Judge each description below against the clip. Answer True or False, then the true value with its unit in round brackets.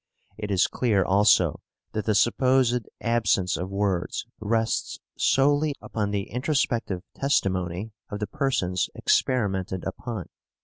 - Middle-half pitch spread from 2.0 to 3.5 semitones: False (4.5 semitones)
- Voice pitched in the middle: False (105 Hz)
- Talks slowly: True (120 wpm)